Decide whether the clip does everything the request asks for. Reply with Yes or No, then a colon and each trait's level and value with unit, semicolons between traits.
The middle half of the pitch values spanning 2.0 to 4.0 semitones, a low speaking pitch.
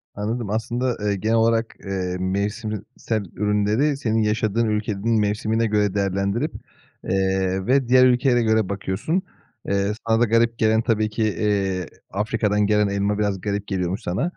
Yes: narrow, 2.4 semitones; low, 105 Hz